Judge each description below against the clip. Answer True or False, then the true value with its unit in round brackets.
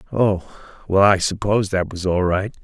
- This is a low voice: True (95 Hz)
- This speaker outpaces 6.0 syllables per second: False (4.9 syllables/s)